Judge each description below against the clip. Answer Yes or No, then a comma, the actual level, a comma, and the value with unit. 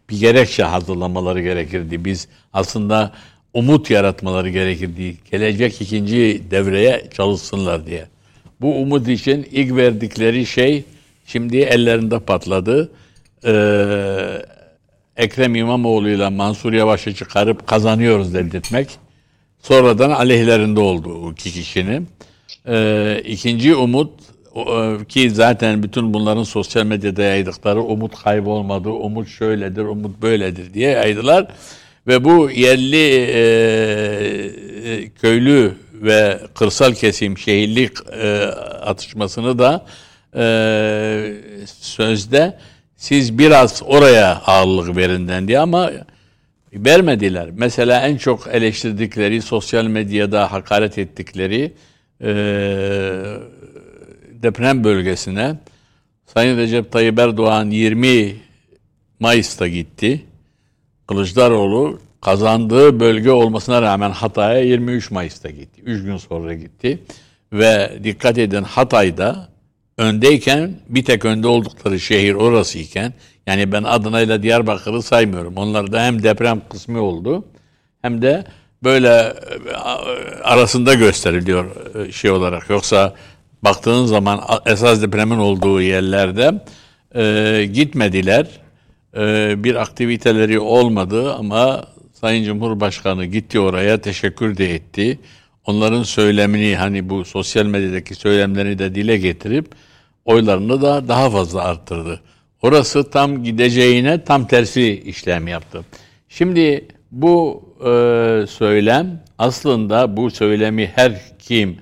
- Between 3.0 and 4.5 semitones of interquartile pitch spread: Yes, average, 3.3 semitones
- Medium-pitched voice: No, low, 110 Hz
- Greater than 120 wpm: No, average, 100 wpm